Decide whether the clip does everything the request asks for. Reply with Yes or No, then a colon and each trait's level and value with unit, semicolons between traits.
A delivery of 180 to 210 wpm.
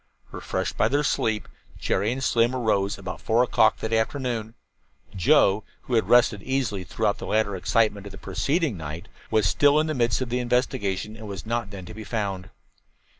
Yes: average, 185 wpm